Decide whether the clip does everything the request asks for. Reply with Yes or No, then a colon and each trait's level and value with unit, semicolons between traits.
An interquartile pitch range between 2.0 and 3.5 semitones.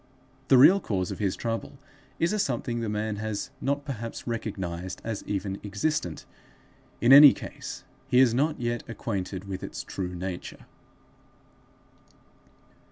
No: average, 4.9 semitones